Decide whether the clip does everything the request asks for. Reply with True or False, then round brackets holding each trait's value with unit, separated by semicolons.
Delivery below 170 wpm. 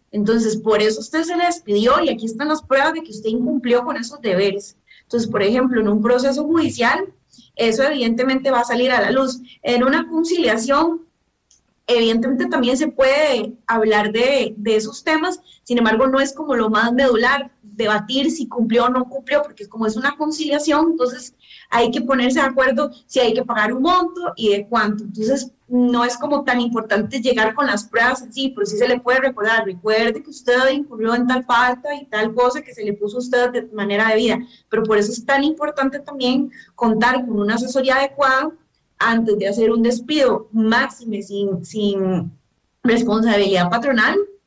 False (190 wpm)